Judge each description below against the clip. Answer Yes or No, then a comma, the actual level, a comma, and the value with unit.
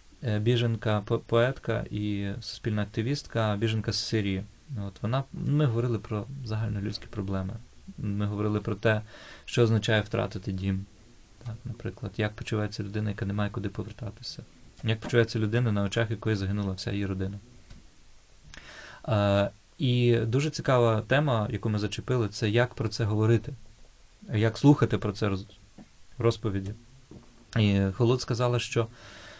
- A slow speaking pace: No, average, 135 wpm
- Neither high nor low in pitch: No, low, 110 Hz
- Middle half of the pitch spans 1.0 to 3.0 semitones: Yes, narrow, 2.4 semitones